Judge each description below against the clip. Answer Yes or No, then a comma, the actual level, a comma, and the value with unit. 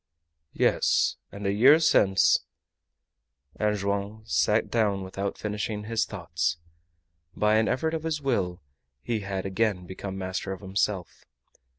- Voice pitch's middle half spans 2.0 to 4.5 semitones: Yes, narrow, 2.6 semitones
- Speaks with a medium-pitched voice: No, low, 100 Hz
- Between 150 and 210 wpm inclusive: No, average, 140 wpm